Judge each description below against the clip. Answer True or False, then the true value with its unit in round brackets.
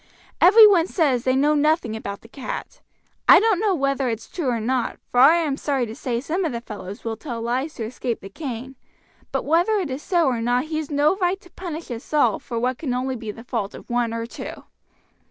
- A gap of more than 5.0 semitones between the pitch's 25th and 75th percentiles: True (5.4 semitones)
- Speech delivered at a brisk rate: True (230 wpm)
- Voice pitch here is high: True (265 Hz)